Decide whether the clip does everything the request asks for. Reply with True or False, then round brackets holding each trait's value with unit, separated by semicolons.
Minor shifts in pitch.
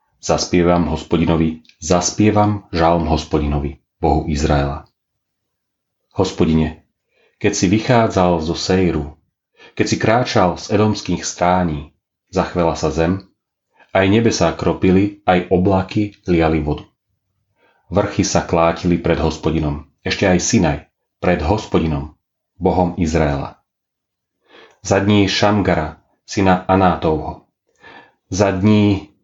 False (3.7 semitones)